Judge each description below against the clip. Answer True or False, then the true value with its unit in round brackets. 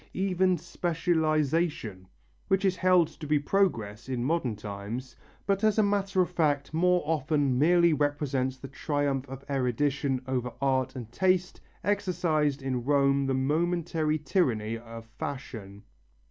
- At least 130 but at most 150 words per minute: True (135 wpm)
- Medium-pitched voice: True (145 Hz)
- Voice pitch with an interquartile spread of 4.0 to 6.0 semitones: True (5.1 semitones)